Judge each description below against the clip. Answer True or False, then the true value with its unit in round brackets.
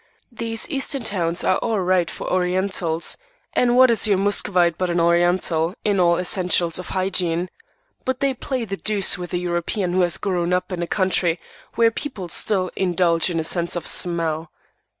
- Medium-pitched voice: True (180 Hz)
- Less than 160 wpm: False (180 wpm)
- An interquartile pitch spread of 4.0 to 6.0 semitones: False (2.9 semitones)